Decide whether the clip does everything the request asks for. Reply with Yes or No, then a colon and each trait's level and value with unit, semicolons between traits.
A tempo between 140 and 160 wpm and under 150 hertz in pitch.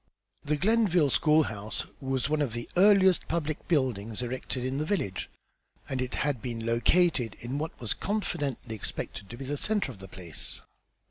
No: average, 175 wpm; low, 135 Hz